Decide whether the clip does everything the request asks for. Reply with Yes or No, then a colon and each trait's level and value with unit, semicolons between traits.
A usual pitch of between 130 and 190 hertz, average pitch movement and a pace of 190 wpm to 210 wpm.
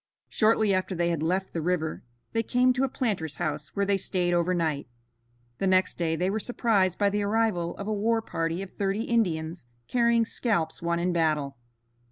Yes: medium, 185 Hz; average, 4.5 semitones; average, 195 wpm